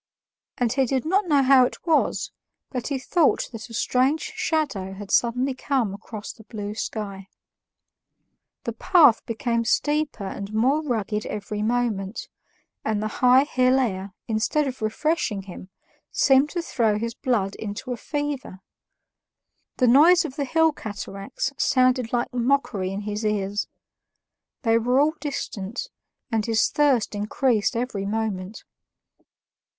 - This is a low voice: No, high, 235 Hz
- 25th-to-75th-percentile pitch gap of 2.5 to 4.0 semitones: No, average, 4.7 semitones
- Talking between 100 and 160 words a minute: Yes, average, 140 wpm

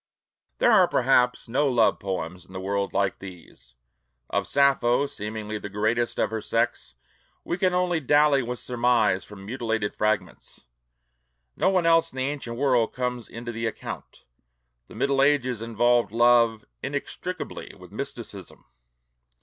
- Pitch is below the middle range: Yes, low, 120 Hz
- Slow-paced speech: No, average, 150 wpm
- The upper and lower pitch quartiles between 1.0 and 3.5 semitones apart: No, average, 4.2 semitones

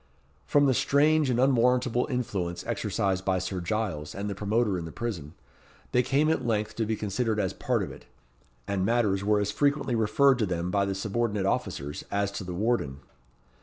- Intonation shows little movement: No, average, 4.3 semitones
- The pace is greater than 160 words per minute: Yes, average, 190 wpm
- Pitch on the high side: No, low, 105 Hz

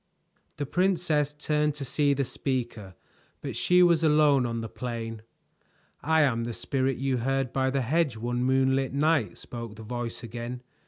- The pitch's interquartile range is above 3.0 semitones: Yes, average, 3.8 semitones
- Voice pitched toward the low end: Yes, low, 130 Hz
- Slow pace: No, average, 165 wpm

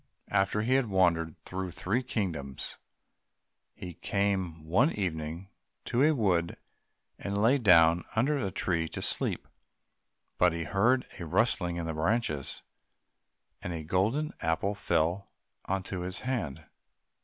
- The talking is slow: Yes, slow, 130 wpm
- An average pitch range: Yes, average, 4.6 semitones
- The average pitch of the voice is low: Yes, very low, 95 Hz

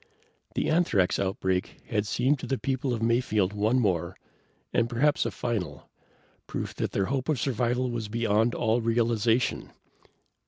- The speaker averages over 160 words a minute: No, average, 150 wpm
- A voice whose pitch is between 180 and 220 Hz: No, low, 115 Hz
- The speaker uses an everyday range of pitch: Yes, average, 3.3 semitones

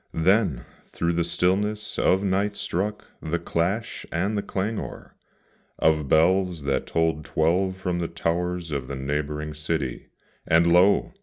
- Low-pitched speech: Yes, very low, 85 Hz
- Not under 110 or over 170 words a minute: Yes, average, 140 wpm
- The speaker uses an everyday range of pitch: Yes, average, 3.5 semitones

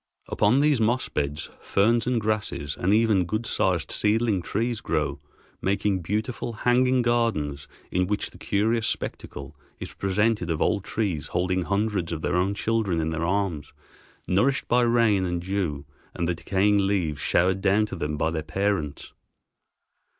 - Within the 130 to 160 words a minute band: Yes, average, 155 wpm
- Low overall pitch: Yes, low, 100 Hz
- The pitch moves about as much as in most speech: Yes, average, 4.6 semitones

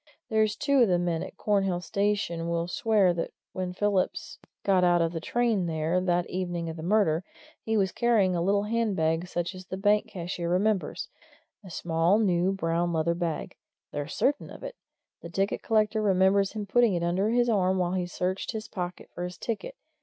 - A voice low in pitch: No, medium, 185 Hz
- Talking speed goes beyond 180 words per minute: Yes, average, 190 wpm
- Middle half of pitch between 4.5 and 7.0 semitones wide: No, average, 3.3 semitones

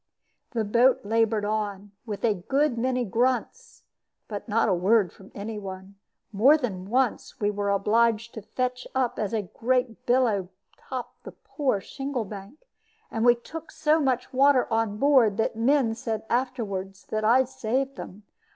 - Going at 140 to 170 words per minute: Yes, average, 165 wpm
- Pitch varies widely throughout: No, average, 3.7 semitones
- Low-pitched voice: No, high, 230 Hz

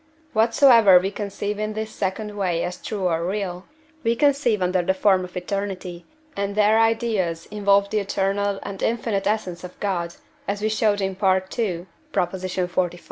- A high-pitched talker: Yes, high, 200 Hz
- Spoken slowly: No, average, 160 wpm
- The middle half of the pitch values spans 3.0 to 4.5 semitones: No, narrow, 2.6 semitones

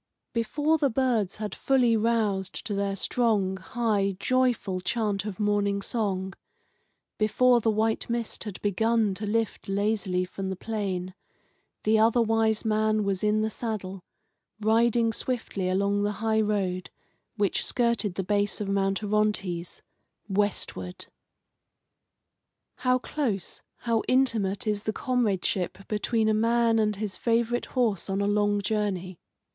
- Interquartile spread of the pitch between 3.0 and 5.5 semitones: No, narrow, 2.6 semitones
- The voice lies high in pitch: Yes, high, 210 Hz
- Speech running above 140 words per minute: No, slow, 135 wpm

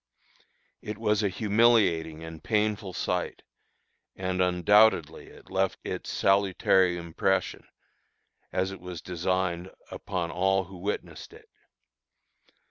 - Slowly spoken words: Yes, slow, 110 wpm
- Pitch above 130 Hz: No, very low, 95 Hz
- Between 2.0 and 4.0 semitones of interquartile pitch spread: Yes, narrow, 2.4 semitones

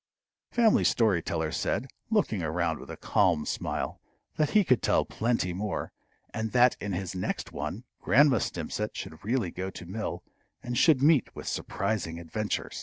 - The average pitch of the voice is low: Yes, low, 105 Hz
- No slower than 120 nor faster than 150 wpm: No, average, 165 wpm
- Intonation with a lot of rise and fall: Yes, wide, 6.0 semitones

